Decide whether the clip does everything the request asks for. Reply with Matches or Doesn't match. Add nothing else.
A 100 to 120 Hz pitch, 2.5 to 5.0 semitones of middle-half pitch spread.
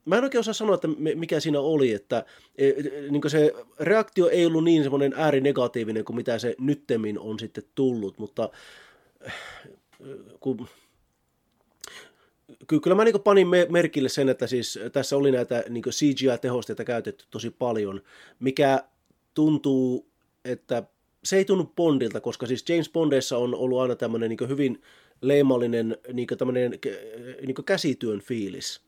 Doesn't match